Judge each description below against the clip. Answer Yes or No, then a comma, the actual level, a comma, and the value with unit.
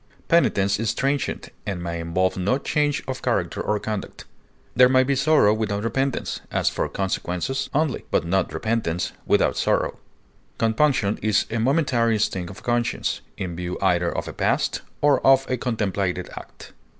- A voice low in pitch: Yes, low, 110 Hz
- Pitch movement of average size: No, wide, 5.8 semitones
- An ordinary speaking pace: Yes, average, 160 wpm